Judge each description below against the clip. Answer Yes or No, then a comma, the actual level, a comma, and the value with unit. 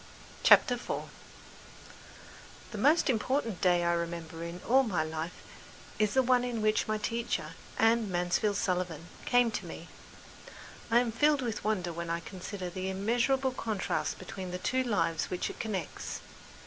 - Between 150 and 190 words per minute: Yes, average, 155 wpm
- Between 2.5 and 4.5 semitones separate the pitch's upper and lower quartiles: No, average, 5.1 semitones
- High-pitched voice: Yes, high, 210 Hz